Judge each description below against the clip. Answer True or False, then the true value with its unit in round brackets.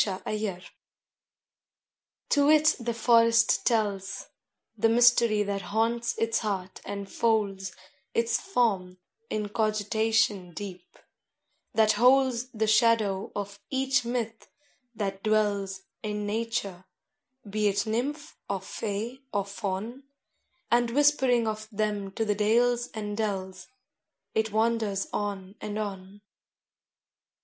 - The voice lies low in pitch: False (215 Hz)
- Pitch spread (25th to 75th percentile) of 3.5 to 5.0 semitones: False (2.6 semitones)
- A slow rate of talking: True (115 wpm)